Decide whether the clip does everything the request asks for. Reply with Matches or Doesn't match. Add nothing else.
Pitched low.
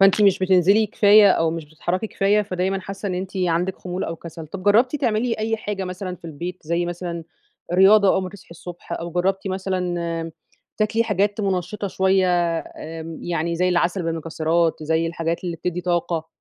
Doesn't match